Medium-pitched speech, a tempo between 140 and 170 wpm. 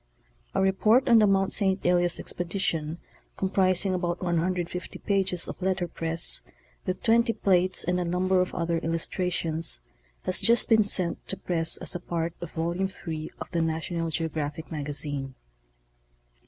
Yes: medium, 175 Hz; average, 155 wpm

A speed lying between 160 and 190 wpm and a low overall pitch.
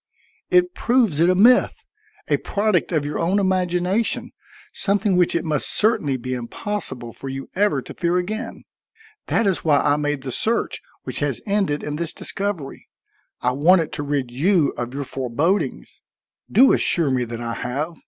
No: average, 170 wpm; medium, 170 Hz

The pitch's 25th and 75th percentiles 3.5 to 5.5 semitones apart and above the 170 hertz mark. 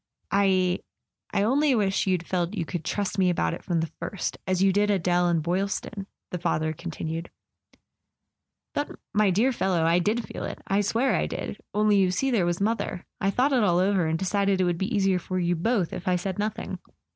No: average, 2.8 semitones; high, 190 Hz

